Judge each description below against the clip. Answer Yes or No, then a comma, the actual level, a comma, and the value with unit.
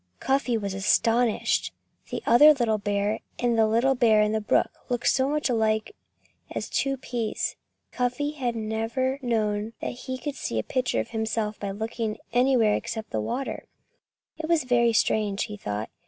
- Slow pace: No, average, 170 wpm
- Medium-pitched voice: No, high, 230 Hz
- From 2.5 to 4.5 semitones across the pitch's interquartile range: Yes, average, 3.1 semitones